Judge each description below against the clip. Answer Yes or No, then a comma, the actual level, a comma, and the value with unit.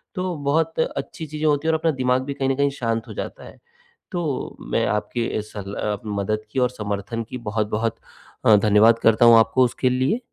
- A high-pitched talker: No, low, 120 Hz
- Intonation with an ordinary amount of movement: Yes, average, 4.8 semitones